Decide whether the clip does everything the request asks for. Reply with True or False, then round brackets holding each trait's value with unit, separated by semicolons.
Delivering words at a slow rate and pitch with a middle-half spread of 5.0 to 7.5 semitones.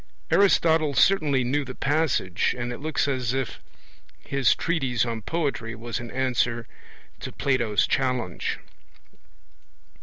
False (120 wpm; 3.6 semitones)